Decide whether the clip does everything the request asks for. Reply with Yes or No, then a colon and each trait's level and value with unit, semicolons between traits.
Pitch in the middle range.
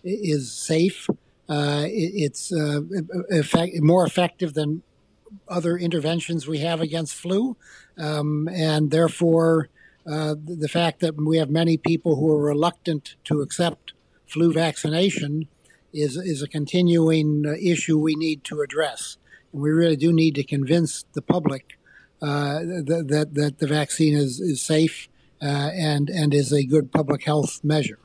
Yes: medium, 160 Hz